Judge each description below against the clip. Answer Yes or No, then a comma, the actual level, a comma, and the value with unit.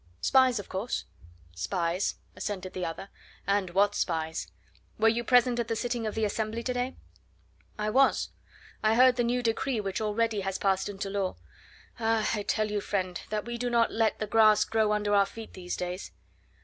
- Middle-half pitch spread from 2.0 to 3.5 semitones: Yes, average, 3.0 semitones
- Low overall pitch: No, high, 215 Hz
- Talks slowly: No, average, 190 wpm